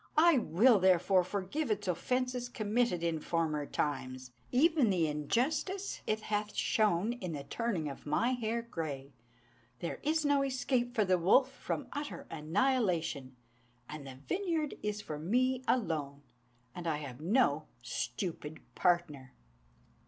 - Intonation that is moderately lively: No, wide, 8.3 semitones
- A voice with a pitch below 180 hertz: No, high, 190 Hz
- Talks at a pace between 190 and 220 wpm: No, slow, 135 wpm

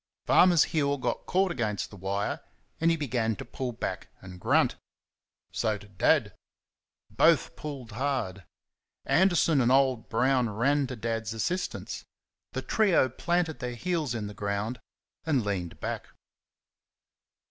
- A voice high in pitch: No, low, 125 Hz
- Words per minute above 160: No, slow, 135 wpm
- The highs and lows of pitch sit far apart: Yes, wide, 5.7 semitones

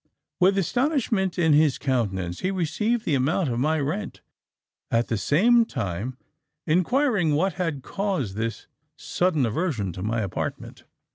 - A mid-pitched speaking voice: Yes, medium, 155 Hz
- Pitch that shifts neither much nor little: No, wide, 8.4 semitones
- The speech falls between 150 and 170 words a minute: No, average, 140 wpm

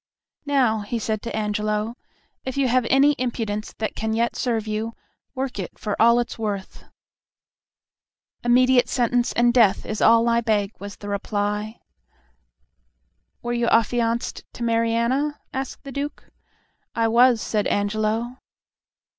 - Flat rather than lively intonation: Yes, narrow, 2.2 semitones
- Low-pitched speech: No, high, 230 Hz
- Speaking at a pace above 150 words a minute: No, average, 140 wpm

